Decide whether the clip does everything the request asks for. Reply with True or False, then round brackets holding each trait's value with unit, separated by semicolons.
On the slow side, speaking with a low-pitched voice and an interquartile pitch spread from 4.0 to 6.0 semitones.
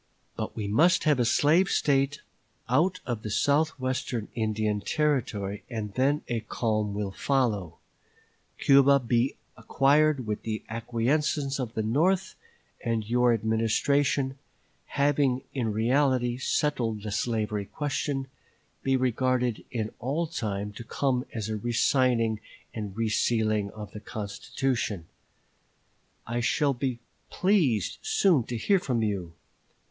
True (130 wpm; 120 Hz; 4.3 semitones)